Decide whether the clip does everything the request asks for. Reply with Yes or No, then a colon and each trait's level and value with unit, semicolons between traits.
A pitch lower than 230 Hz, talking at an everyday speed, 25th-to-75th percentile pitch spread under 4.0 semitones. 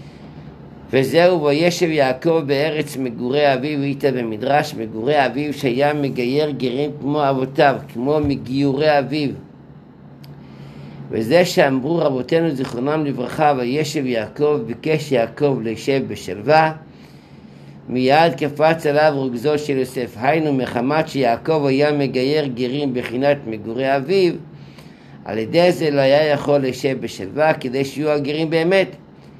Yes: medium, 140 Hz; average, 115 wpm; average, 3.1 semitones